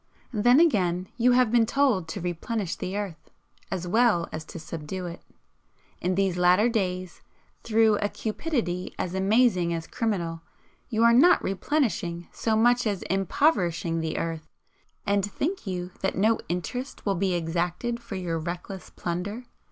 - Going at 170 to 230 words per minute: No, average, 150 wpm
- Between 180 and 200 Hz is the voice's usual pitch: Yes, high, 190 Hz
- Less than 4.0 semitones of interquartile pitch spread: No, average, 4.7 semitones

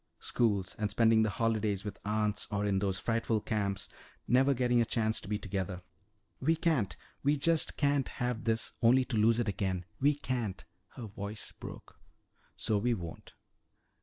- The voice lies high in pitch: No, low, 110 Hz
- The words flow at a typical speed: Yes, average, 165 wpm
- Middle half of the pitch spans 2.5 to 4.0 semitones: Yes, average, 3.3 semitones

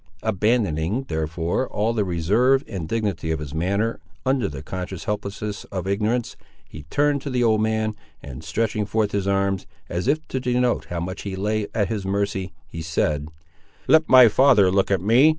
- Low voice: Yes, low, 100 Hz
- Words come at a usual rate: Yes, average, 180 wpm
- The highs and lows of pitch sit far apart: No, average, 4.1 semitones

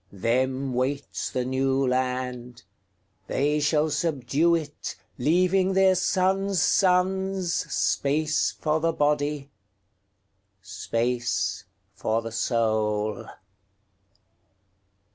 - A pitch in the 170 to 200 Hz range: No, low, 135 Hz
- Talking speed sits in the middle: No, slow, 65 wpm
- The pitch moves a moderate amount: No, wide, 5.9 semitones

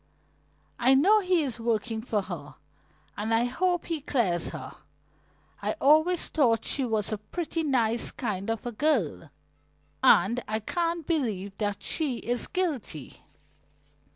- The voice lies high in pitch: Yes, high, 240 Hz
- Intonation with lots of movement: Yes, wide, 6.5 semitones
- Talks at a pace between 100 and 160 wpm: Yes, average, 140 wpm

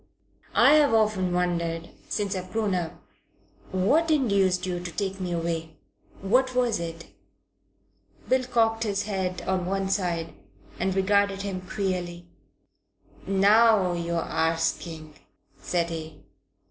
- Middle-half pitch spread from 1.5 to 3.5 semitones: Yes, average, 3.2 semitones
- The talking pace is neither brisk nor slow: No, slow, 120 wpm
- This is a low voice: No, medium, 185 Hz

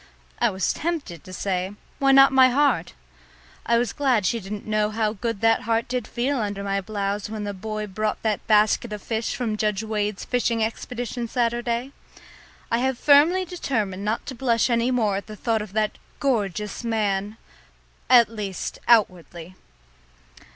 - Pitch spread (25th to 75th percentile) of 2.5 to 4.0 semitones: Yes, average, 2.8 semitones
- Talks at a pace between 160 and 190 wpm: Yes, average, 165 wpm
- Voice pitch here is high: Yes, high, 220 Hz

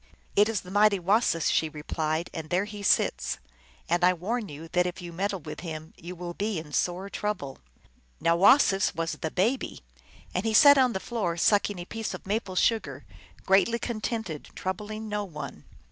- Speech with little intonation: No, average, 4.1 semitones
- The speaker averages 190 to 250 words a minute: Yes, average, 195 wpm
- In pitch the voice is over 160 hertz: Yes, high, 190 Hz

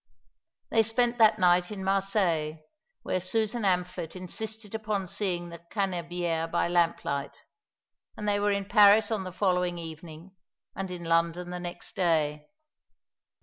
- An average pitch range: Yes, average, 3.2 semitones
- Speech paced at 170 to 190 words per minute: No, average, 140 wpm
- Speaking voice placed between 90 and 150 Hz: No, medium, 180 Hz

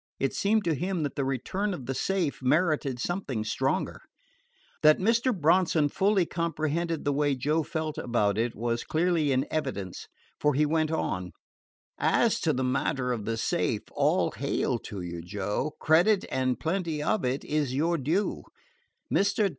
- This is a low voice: No, medium, 150 Hz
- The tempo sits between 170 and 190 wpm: No, average, 160 wpm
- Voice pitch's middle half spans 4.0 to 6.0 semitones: Yes, average, 5.1 semitones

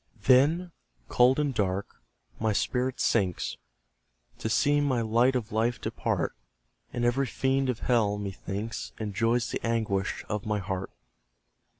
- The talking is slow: Yes, slow, 130 wpm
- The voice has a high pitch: No, low, 115 Hz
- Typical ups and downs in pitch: Yes, average, 3.6 semitones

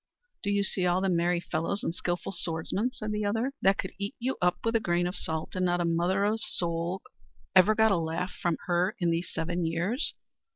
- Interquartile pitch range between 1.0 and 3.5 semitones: Yes, average, 2.9 semitones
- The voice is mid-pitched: Yes, medium, 180 Hz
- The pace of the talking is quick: Yes, fast, 220 wpm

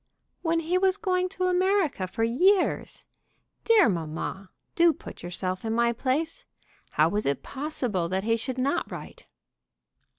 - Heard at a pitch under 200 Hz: No, very high, 270 Hz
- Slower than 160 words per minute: Yes, average, 145 wpm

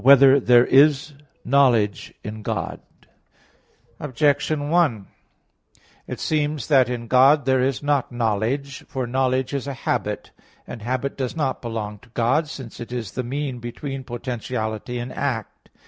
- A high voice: No, low, 130 Hz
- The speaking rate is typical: Yes, average, 150 wpm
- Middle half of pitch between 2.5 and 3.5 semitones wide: Yes, average, 2.8 semitones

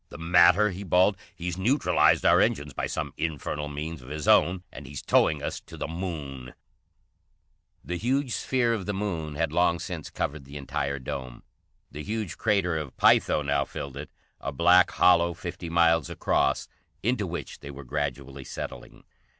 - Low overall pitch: Yes, very low, 80 Hz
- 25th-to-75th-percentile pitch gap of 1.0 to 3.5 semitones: No, average, 4.3 semitones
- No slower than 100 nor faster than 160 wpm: No, average, 170 wpm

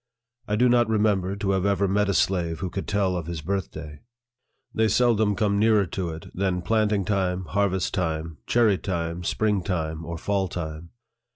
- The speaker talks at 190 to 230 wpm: No, average, 180 wpm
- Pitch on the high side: No, very low, 95 Hz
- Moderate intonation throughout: Yes, average, 3.3 semitones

